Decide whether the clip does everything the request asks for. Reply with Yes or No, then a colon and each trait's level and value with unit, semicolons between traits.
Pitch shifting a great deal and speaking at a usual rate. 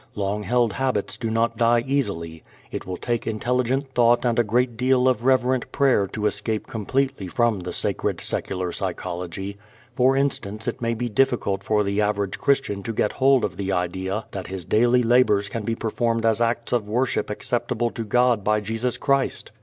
No: average, 3.5 semitones; average, 185 wpm